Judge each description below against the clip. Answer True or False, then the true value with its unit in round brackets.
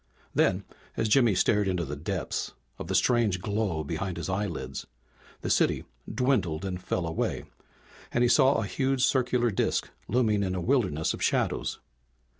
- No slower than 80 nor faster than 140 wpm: False (160 wpm)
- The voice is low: True (100 Hz)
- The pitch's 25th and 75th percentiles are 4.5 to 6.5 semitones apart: True (5.1 semitones)